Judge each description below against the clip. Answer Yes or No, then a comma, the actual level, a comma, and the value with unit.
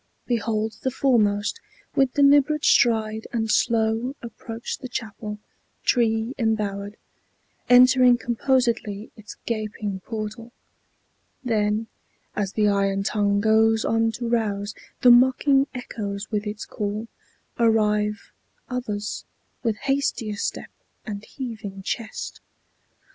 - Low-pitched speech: No, high, 220 Hz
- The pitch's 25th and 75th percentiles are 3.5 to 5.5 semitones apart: No, narrow, 2.5 semitones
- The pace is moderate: No, slow, 105 wpm